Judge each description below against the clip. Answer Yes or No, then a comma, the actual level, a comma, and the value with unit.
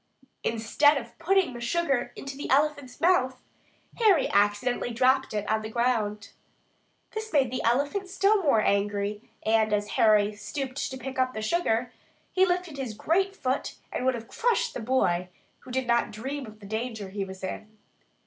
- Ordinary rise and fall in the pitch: Yes, average, 5.0 semitones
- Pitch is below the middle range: No, very high, 250 Hz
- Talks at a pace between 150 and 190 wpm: Yes, average, 175 wpm